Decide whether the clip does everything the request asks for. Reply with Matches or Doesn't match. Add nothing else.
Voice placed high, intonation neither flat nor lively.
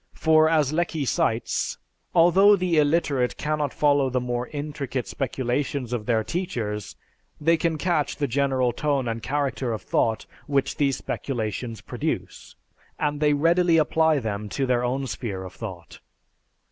Doesn't match